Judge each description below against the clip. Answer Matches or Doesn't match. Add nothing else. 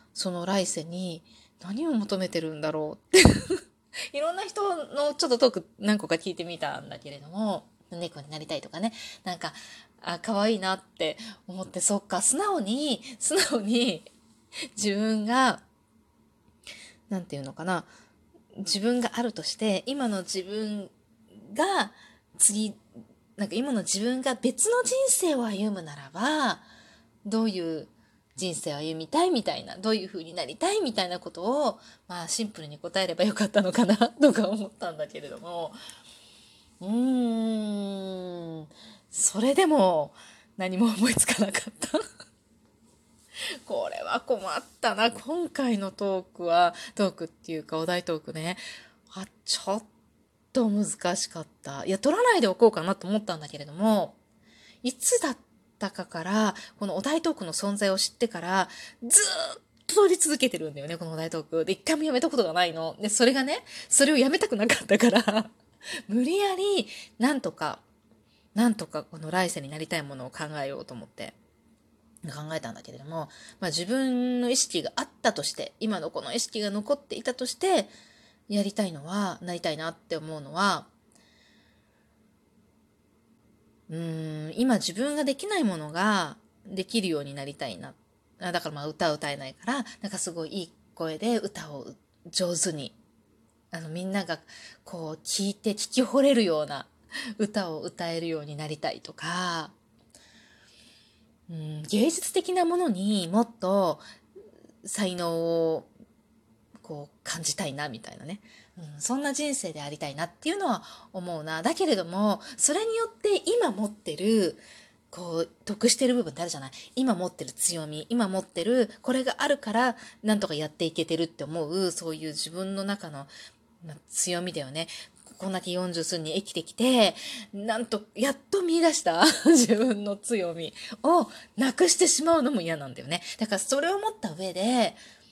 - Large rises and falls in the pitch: Matches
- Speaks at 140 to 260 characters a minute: Doesn't match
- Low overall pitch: Doesn't match